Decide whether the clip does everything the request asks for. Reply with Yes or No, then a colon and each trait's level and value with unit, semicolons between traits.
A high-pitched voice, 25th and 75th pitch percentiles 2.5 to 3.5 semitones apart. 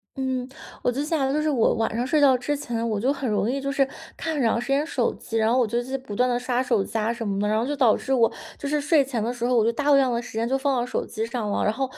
Yes: very high, 250 Hz; average, 3.2 semitones